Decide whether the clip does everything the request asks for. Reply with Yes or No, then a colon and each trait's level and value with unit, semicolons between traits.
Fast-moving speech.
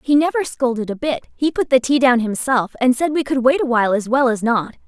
Yes: fast, 260 wpm